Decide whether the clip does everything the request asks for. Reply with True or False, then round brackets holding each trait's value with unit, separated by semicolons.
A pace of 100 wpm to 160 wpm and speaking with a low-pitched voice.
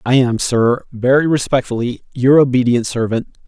True (140 wpm; 125 Hz)